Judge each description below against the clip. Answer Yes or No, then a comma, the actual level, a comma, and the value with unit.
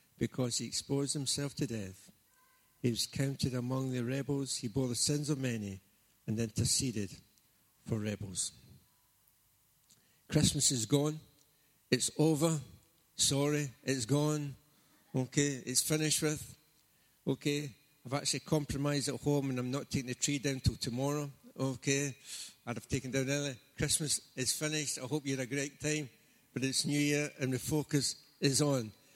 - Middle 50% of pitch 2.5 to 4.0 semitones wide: Yes, average, 2.8 semitones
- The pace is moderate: Yes, average, 150 wpm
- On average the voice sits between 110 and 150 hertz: Yes, medium, 140 Hz